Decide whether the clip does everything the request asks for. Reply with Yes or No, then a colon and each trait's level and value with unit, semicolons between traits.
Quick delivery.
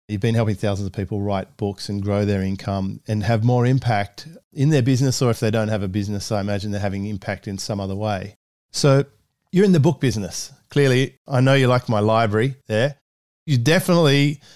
Yes: fast, 210 wpm